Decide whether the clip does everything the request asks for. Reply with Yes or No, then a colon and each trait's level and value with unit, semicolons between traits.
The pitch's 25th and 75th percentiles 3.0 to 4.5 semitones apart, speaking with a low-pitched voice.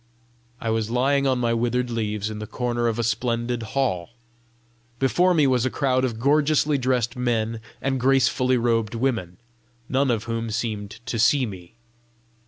No: narrow, 2.5 semitones; low, 120 Hz